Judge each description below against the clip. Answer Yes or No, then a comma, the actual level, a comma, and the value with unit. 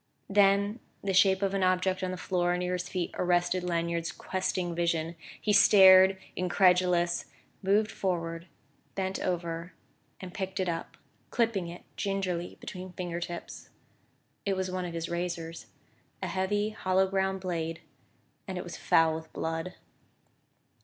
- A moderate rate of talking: Yes, average, 145 wpm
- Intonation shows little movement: Yes, narrow, 1.8 semitones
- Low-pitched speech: No, medium, 180 Hz